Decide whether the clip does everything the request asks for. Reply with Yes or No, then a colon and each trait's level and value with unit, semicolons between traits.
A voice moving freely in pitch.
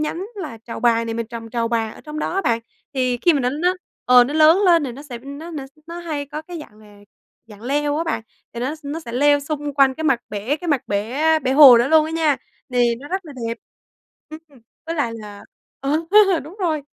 No: average, 4.8 semitones